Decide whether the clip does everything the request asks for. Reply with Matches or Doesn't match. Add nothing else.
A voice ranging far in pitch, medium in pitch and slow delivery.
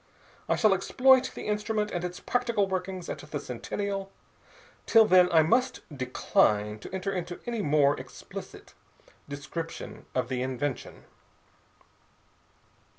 Matches